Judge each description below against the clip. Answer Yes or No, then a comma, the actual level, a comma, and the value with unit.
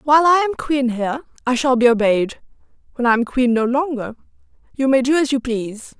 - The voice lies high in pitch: Yes, very high, 255 Hz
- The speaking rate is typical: No, fast, 210 wpm